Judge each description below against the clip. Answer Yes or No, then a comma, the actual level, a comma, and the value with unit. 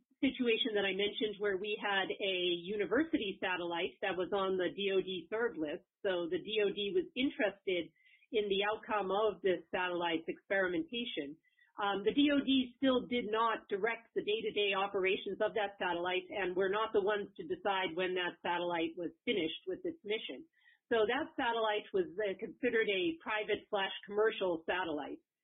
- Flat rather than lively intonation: No, average, 3.9 semitones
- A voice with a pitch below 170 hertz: No, high, 210 Hz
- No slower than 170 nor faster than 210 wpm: No, average, 160 wpm